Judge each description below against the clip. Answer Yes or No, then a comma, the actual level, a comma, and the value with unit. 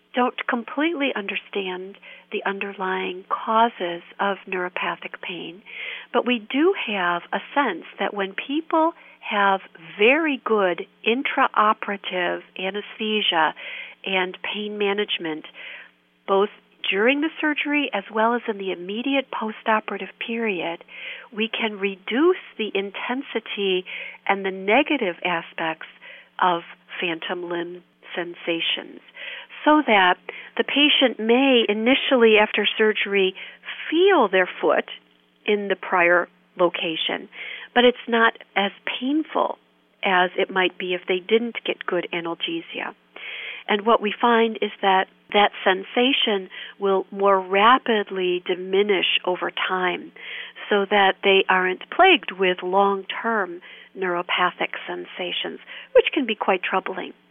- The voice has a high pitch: Yes, high, 200 Hz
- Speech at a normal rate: No, slow, 115 wpm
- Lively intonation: No, average, 4.2 semitones